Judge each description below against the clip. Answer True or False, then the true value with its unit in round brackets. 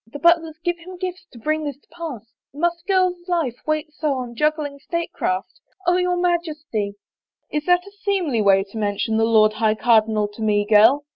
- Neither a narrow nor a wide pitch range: False (7.7 semitones)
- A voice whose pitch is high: True (295 Hz)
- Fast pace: True (220 wpm)